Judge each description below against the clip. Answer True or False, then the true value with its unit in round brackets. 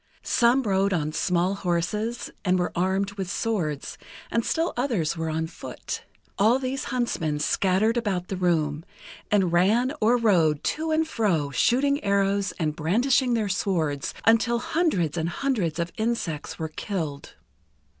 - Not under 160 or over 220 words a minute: False (145 wpm)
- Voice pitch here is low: False (195 Hz)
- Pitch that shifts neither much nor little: False (5.9 semitones)